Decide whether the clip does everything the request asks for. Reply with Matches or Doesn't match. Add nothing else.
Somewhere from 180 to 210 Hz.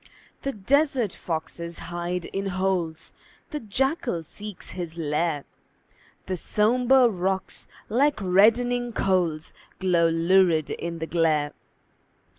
Matches